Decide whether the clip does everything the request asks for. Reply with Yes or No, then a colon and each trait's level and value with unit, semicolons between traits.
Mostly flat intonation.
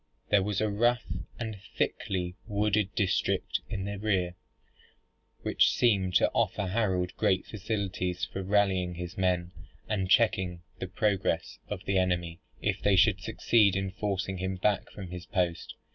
Yes: narrow, 2.3 semitones